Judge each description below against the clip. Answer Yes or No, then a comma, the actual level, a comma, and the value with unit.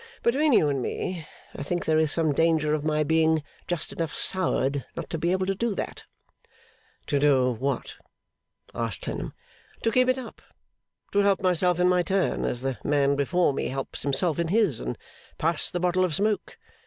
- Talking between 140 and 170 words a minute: No, average, 190 wpm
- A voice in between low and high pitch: Yes, medium, 165 Hz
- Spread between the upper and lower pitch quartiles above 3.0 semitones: Yes, average, 4.5 semitones